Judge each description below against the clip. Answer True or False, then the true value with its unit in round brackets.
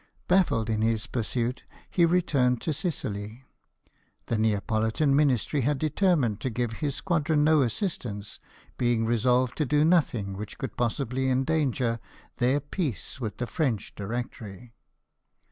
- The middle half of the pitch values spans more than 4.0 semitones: True (4.8 semitones)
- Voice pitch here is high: False (125 Hz)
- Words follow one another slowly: True (130 wpm)